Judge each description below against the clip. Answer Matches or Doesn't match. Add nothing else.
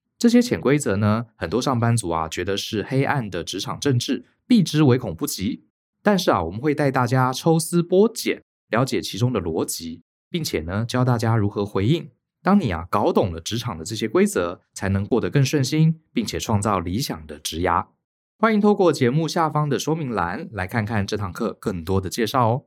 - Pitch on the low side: Matches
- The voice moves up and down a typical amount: Doesn't match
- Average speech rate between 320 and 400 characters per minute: Doesn't match